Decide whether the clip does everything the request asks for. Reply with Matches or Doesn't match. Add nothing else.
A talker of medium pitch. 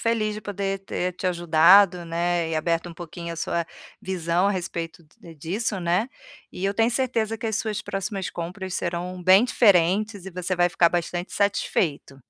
Matches